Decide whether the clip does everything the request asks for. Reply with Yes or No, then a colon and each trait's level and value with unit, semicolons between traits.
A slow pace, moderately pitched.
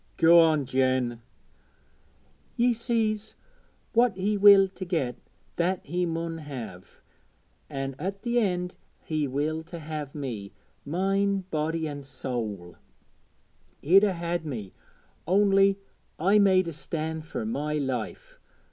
Yes: slow, 125 wpm; medium, 165 Hz